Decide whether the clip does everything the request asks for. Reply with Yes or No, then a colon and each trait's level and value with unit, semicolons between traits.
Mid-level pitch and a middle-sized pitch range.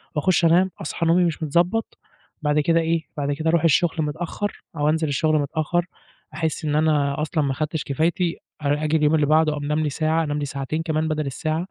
No: medium, 155 Hz; narrow, 2.0 semitones